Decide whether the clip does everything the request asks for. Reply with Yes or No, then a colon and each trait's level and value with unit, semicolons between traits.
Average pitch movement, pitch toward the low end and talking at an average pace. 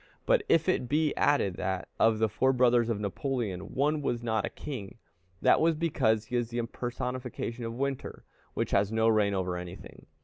Yes: average, 4.1 semitones; low, 120 Hz; average, 190 wpm